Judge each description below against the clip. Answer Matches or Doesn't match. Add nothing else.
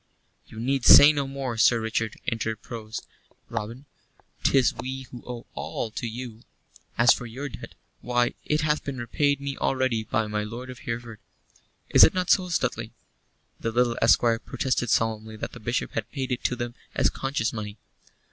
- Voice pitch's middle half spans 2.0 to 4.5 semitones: Matches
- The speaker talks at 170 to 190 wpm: Matches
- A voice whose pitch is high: Doesn't match